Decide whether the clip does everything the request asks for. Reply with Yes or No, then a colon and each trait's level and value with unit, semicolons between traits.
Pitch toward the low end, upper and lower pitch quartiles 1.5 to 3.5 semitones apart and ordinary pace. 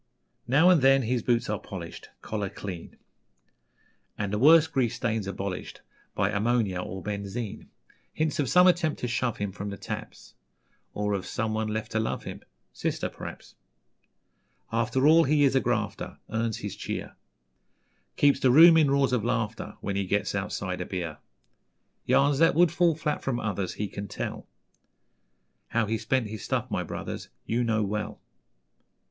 No: low, 115 Hz; average, 4.9 semitones; average, 165 wpm